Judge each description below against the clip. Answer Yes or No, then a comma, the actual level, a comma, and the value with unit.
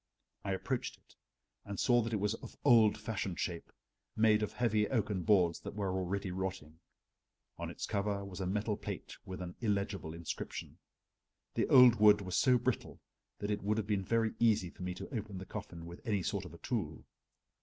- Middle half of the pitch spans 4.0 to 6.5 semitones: No, average, 2.8 semitones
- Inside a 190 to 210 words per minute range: Yes, average, 195 wpm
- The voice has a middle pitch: No, low, 100 Hz